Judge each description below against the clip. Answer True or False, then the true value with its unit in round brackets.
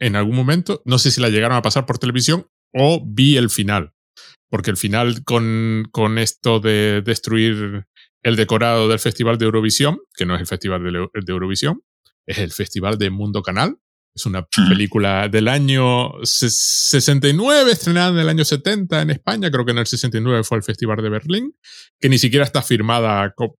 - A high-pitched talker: False (115 Hz)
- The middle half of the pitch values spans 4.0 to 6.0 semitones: True (4.3 semitones)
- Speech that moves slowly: False (185 wpm)